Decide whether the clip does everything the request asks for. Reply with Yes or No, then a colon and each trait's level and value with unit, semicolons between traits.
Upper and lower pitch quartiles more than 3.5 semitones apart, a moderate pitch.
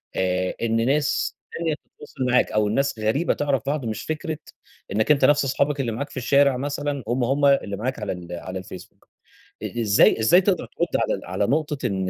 No: average, 5.0 semitones; low, 130 Hz